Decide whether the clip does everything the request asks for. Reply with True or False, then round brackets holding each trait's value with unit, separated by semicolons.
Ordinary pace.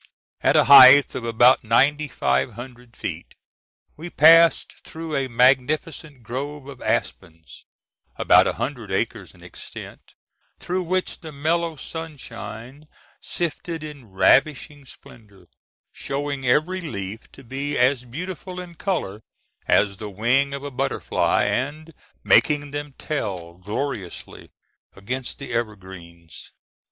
False (125 wpm)